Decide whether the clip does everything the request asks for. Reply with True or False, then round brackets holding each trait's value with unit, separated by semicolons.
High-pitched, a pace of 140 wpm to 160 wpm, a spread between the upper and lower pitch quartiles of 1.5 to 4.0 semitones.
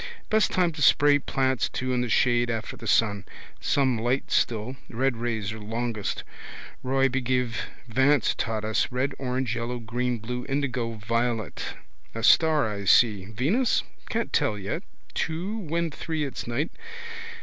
False (125 Hz; 150 wpm; 3.5 semitones)